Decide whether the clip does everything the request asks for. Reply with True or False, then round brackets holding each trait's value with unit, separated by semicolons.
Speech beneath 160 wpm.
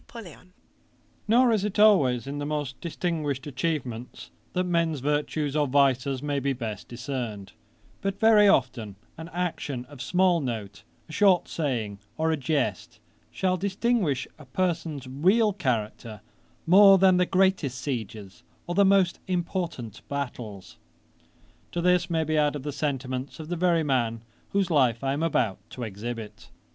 True (150 wpm)